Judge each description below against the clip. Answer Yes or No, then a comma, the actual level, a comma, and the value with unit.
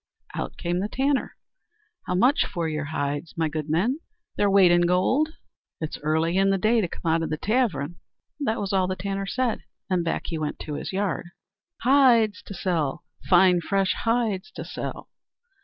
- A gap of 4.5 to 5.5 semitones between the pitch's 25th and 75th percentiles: Yes, average, 4.8 semitones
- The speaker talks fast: No, average, 185 wpm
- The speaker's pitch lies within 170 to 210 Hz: Yes, medium, 185 Hz